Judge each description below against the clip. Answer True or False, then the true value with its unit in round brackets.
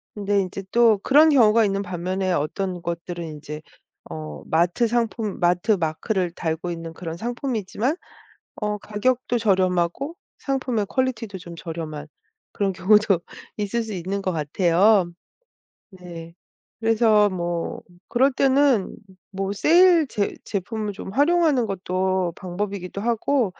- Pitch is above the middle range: True (195 Hz)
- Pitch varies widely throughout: False (4.7 semitones)